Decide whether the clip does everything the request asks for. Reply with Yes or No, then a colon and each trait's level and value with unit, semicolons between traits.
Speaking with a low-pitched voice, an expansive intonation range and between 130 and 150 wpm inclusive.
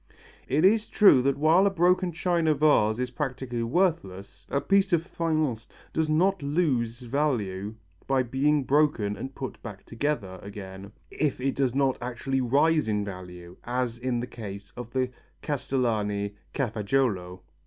Yes: low, 130 Hz; wide, 5.8 semitones; average, 145 wpm